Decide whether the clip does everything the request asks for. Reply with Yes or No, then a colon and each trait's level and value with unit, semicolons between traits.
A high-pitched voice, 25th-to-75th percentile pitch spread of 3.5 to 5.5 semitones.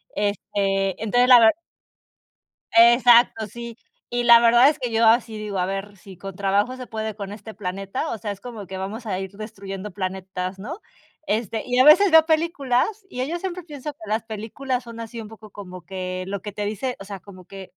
Yes: high, 220 Hz; average, 3.8 semitones